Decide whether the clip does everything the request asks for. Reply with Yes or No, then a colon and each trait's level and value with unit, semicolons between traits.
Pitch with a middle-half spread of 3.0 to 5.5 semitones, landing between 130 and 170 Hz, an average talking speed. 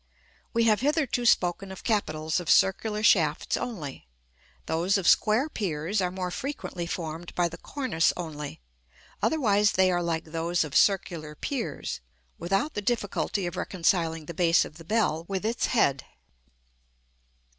No: average, 4.6 semitones; medium, 180 Hz; average, 145 wpm